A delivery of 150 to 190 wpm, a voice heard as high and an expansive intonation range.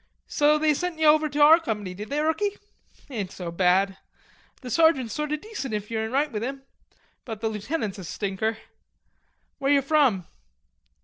Yes: average, 180 wpm; very high, 265 Hz; wide, 6.4 semitones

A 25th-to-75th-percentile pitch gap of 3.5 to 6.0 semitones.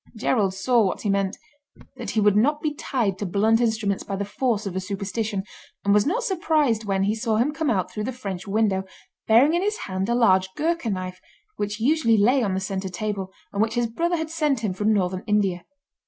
Yes: average, 4.6 semitones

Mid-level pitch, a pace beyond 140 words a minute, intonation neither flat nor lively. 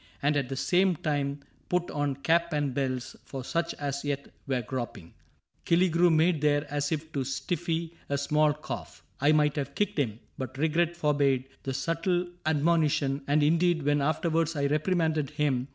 Yes: medium, 150 Hz; average, 170 wpm; average, 3.0 semitones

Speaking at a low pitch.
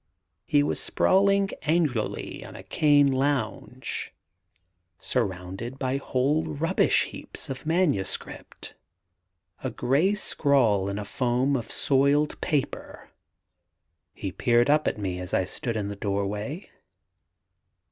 Yes: low, 130 Hz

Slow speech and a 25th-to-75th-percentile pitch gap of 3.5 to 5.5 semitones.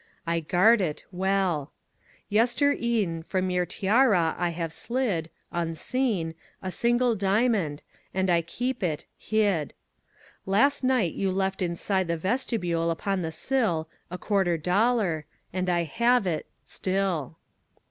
Yes: slow, 125 wpm; average, 5.0 semitones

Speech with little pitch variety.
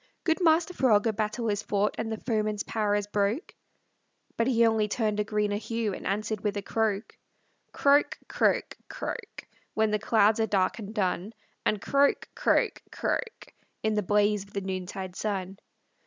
Yes: narrow, 1.7 semitones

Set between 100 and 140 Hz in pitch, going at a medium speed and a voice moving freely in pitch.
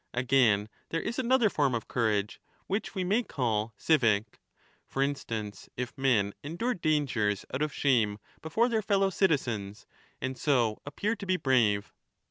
Yes: low, 135 Hz; average, 155 wpm; wide, 8.5 semitones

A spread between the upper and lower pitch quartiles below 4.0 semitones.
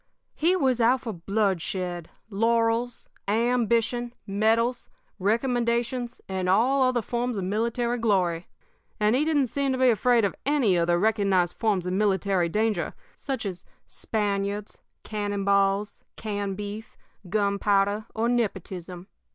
Yes: average, 3.4 semitones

